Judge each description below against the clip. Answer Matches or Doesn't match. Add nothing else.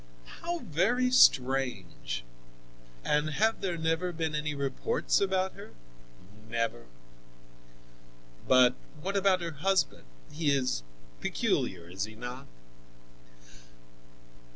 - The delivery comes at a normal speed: Doesn't match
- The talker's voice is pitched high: Doesn't match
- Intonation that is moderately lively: Doesn't match